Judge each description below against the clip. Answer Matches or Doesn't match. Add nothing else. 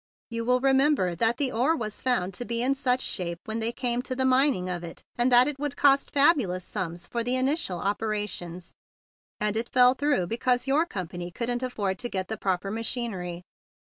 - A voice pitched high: Matches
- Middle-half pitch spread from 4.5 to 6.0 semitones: Matches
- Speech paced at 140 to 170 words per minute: Doesn't match